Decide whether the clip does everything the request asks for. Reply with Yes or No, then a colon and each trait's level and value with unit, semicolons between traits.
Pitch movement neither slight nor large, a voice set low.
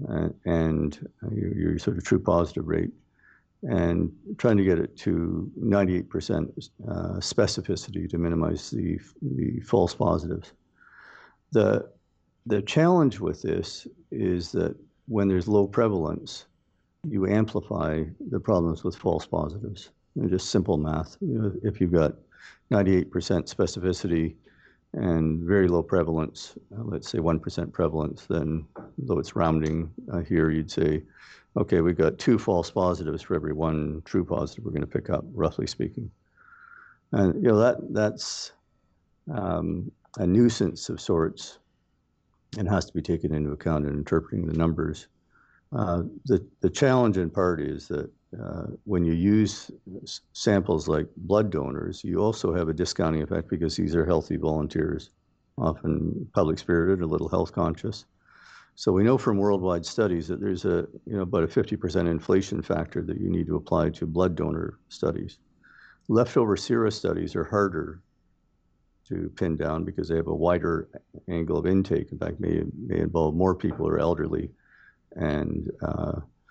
Yes: average, 3.5 semitones; very low, 85 Hz